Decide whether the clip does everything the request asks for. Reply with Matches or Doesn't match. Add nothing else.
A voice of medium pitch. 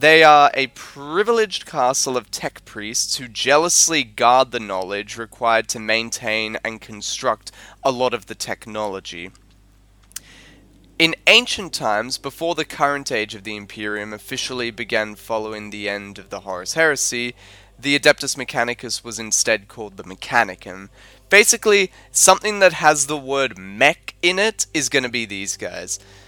Doesn't match